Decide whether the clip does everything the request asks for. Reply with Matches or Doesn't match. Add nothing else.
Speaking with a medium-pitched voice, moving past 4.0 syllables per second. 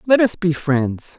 Doesn't match